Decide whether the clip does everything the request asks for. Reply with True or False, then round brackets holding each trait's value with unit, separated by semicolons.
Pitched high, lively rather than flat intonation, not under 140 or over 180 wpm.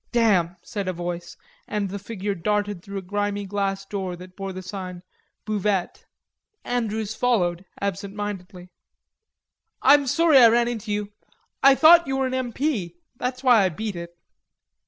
False (205 Hz; 4.2 semitones; 155 wpm)